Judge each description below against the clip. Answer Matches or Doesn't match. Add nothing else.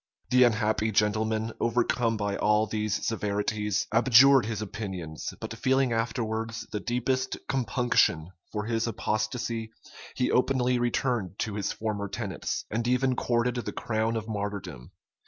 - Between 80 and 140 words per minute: Matches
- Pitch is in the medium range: Doesn't match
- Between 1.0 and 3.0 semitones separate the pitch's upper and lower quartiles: Matches